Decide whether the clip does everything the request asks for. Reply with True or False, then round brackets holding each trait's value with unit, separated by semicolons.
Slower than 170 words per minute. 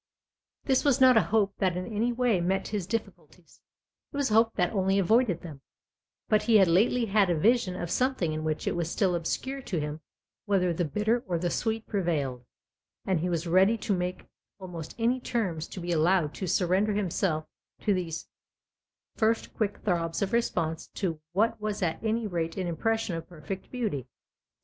False (190 wpm)